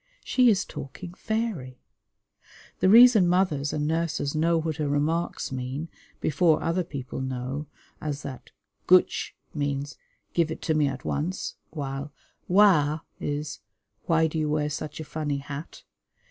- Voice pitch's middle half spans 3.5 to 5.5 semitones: No, average, 3.0 semitones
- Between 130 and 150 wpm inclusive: Yes, average, 145 wpm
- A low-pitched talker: No, medium, 155 Hz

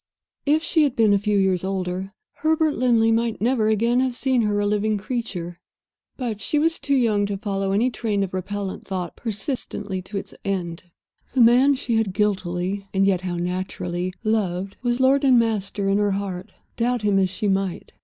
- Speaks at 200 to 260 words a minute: No, average, 190 wpm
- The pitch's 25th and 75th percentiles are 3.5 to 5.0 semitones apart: Yes, average, 3.8 semitones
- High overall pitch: Yes, high, 205 Hz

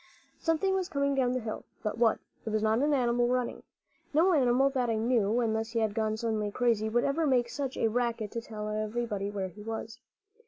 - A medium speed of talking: No, fast, 210 wpm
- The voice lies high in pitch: Yes, high, 235 Hz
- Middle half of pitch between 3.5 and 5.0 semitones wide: No, average, 2.8 semitones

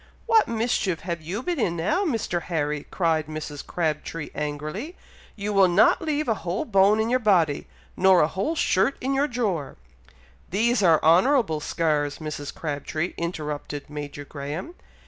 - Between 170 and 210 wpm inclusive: No, average, 155 wpm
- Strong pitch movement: Yes, wide, 6.4 semitones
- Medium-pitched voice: Yes, medium, 175 Hz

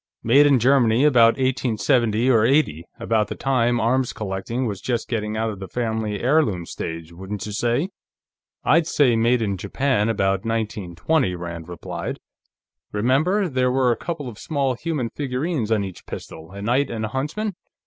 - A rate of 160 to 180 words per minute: Yes, average, 170 wpm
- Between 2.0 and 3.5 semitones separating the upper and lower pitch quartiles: No, average, 4.1 semitones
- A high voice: No, low, 115 Hz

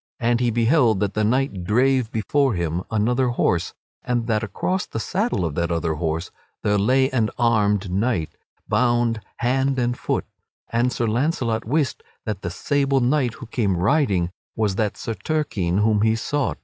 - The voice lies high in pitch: No, low, 115 Hz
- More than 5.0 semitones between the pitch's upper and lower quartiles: No, average, 4.0 semitones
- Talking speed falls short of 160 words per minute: No, average, 170 wpm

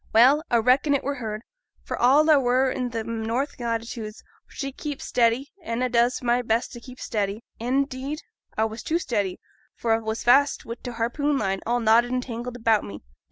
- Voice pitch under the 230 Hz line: No, high, 240 Hz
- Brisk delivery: Yes, fast, 210 wpm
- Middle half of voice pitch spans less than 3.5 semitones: Yes, narrow, 2.6 semitones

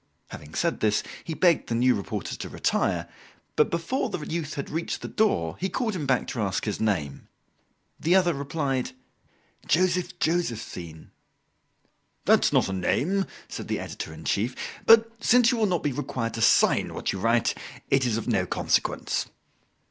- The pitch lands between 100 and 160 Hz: Yes, medium, 140 Hz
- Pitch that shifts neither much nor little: No, wide, 8.1 semitones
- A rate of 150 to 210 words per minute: Yes, average, 170 wpm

